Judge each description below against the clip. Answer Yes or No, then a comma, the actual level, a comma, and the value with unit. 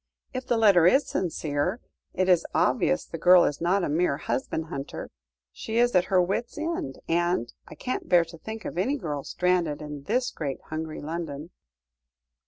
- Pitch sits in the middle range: Yes, medium, 175 Hz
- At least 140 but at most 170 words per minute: No, average, 180 wpm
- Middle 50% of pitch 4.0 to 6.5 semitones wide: Yes, average, 4.5 semitones